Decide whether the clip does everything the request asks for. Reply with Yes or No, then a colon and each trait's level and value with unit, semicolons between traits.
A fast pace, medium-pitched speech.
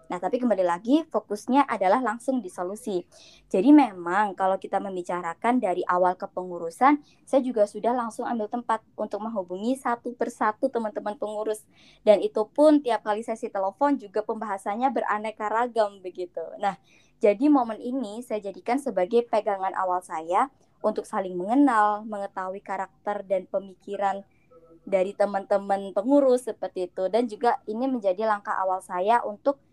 No: fast, 145 wpm; high, 210 Hz